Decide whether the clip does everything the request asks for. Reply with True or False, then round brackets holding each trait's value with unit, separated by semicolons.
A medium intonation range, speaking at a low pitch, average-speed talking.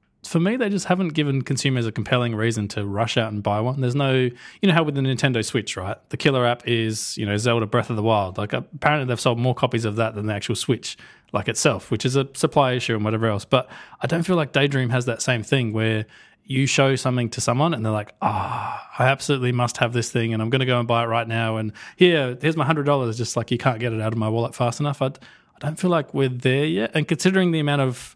False (4.0 semitones; 125 Hz; 270 wpm)